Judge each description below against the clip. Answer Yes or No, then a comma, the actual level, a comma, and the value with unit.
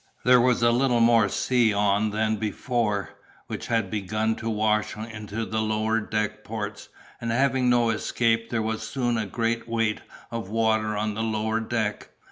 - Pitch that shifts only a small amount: Yes, narrow, 1.5 semitones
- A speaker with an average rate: Yes, average, 170 wpm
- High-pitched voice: No, low, 110 Hz